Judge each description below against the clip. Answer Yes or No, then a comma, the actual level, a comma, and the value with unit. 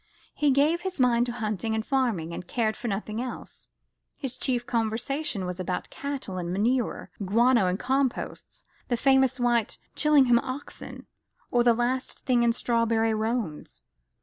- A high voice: Yes, high, 240 Hz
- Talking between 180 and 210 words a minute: No, average, 150 wpm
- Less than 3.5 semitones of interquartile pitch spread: Yes, average, 3.0 semitones